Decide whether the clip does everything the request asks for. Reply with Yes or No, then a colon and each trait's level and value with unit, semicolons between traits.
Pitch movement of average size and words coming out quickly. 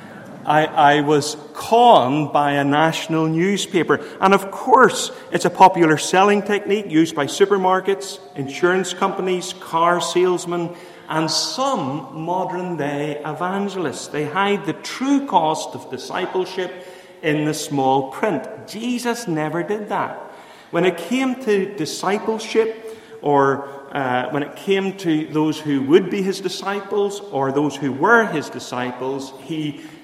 No: average, 4.7 semitones; slow, 135 wpm